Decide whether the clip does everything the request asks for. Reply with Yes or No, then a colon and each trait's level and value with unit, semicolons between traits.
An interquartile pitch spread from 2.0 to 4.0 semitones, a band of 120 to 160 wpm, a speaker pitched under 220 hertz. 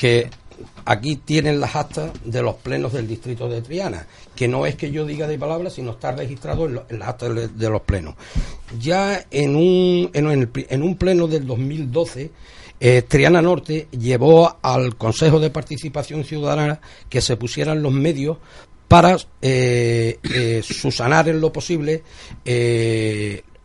No: average, 4.6 semitones; average, 150 wpm; medium, 140 Hz